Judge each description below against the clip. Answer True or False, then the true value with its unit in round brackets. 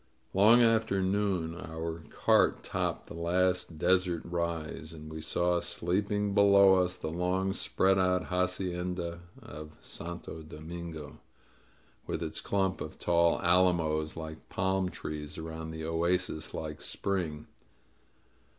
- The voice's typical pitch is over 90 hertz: False (85 Hz)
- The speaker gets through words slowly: True (125 wpm)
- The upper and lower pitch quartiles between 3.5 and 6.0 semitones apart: False (2.6 semitones)